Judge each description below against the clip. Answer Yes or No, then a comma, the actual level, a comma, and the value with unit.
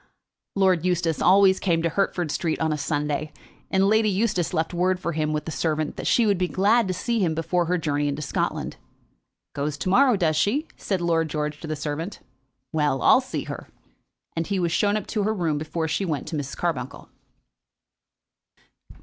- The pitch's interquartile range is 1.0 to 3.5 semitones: No, average, 3.9 semitones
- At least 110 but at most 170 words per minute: No, average, 195 wpm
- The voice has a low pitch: No, medium, 170 Hz